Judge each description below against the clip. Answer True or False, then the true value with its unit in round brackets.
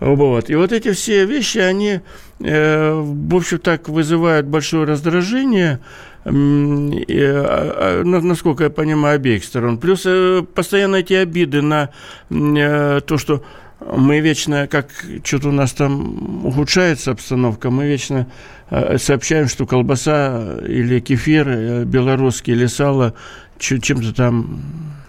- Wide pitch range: False (3.7 semitones)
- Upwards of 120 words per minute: False (110 wpm)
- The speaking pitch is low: False (145 Hz)